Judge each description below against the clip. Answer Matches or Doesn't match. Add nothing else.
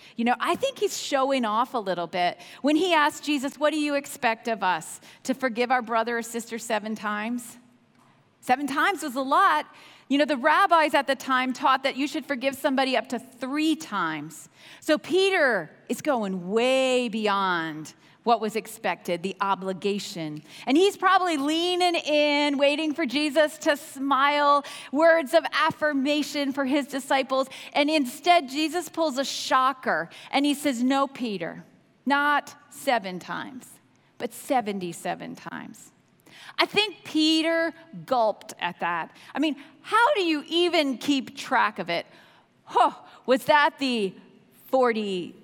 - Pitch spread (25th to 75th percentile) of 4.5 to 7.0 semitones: Matches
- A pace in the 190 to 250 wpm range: Doesn't match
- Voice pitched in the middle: Doesn't match